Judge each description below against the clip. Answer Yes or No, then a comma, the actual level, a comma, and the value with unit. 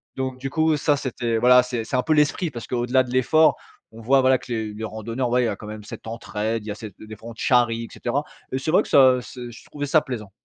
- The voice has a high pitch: No, low, 125 Hz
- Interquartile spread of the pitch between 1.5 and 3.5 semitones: Yes, average, 2.8 semitones